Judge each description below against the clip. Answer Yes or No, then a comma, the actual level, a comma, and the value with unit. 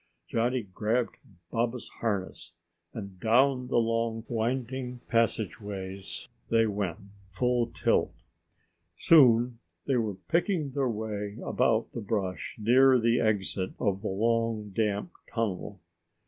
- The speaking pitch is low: Yes, low, 115 Hz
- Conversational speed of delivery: No, slow, 115 wpm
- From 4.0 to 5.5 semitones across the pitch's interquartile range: No, average, 3.2 semitones